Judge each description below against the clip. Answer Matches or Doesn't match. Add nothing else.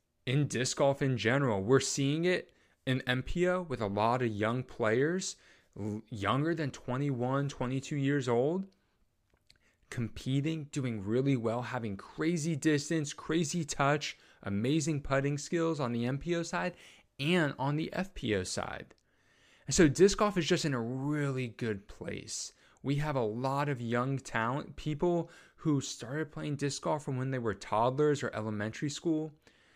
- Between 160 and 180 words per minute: Doesn't match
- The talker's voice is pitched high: Doesn't match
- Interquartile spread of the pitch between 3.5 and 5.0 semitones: Matches